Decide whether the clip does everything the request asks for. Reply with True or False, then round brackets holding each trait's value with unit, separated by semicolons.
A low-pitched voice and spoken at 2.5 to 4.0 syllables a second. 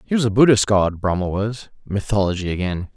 False (105 Hz; 5.6 syllables/s)